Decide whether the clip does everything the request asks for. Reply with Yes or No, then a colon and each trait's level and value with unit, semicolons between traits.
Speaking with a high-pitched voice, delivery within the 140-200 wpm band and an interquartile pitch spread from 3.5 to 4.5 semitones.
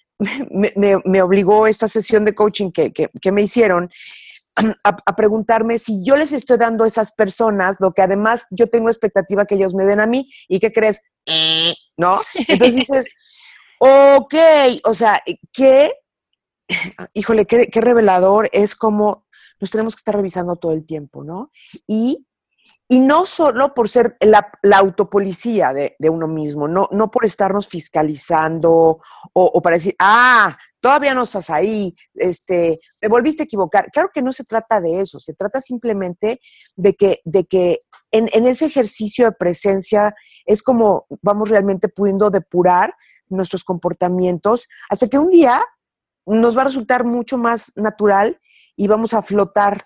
Yes: high, 210 Hz; average, 165 wpm; average, 3.8 semitones